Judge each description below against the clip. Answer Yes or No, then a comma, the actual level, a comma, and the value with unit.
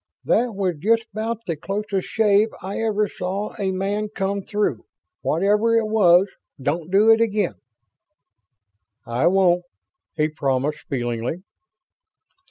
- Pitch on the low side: No, high, 195 Hz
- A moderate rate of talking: No, slow, 125 wpm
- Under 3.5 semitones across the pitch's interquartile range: No, average, 3.8 semitones